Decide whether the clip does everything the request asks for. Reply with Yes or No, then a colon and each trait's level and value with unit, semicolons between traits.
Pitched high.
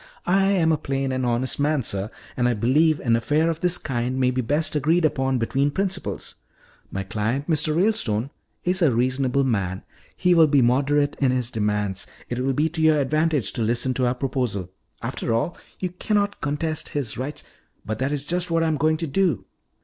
No: medium, 140 Hz